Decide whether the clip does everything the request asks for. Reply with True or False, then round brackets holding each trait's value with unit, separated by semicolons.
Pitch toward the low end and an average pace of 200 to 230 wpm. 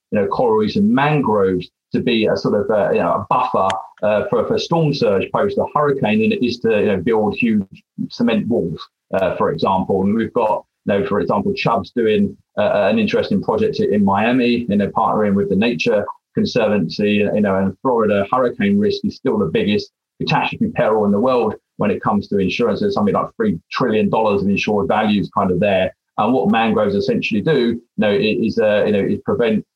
False (145 Hz; 205 wpm)